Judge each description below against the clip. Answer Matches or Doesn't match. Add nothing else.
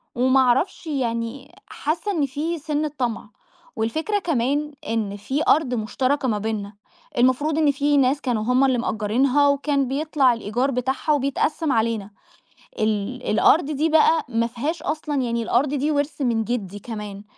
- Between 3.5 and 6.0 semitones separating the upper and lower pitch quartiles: Matches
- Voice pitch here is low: Doesn't match